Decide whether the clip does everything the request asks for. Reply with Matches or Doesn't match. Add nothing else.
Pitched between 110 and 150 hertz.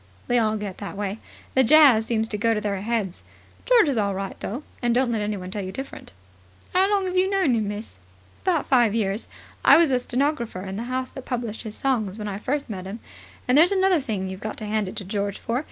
Doesn't match